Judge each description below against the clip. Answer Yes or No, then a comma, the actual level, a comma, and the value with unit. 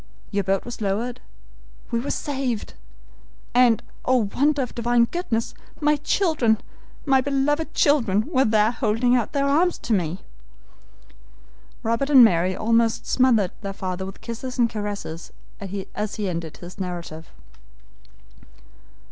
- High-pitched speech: Yes, high, 230 Hz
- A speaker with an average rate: No, slow, 130 wpm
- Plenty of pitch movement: No, average, 4.9 semitones